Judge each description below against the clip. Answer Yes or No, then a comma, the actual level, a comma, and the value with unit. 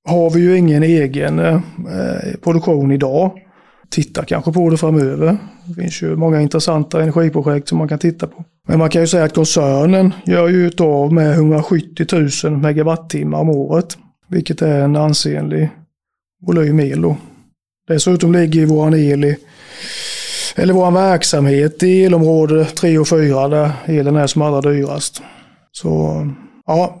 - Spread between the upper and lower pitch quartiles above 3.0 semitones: No, narrow, 2.6 semitones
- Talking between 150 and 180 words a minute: Yes, average, 155 wpm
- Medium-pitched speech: Yes, medium, 160 Hz